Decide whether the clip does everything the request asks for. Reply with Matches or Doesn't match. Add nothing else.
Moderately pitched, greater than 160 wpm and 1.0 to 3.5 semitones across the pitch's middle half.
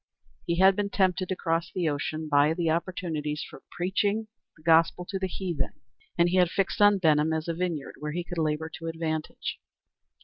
Matches